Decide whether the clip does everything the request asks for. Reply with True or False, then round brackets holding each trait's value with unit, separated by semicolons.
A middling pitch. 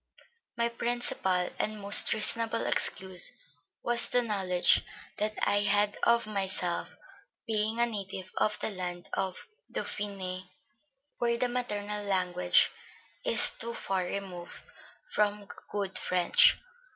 False (205 Hz)